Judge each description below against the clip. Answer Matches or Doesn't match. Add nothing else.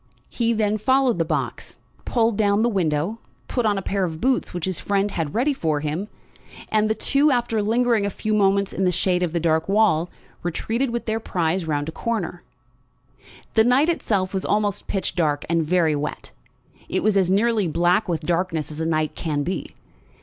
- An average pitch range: Matches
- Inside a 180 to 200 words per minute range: Matches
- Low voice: Doesn't match